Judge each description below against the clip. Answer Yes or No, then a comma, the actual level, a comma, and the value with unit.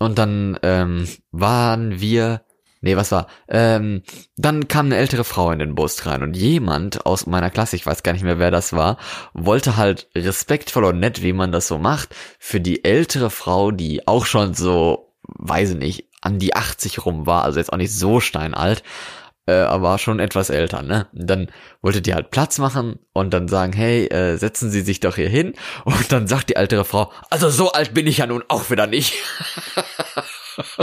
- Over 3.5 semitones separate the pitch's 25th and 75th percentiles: Yes, average, 4.7 semitones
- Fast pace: Yes, fast, 195 wpm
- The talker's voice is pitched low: Yes, low, 100 Hz